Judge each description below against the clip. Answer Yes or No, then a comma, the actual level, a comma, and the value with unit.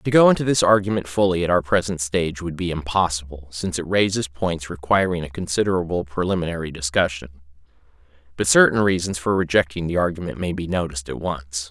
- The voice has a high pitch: No, very low, 85 Hz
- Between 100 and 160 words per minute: No, average, 175 wpm